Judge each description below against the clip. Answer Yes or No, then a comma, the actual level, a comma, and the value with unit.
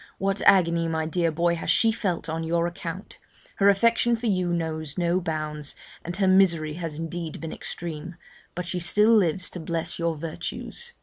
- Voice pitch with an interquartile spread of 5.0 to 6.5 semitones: No, average, 2.7 semitones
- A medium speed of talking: Yes, average, 180 wpm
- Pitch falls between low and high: Yes, medium, 170 Hz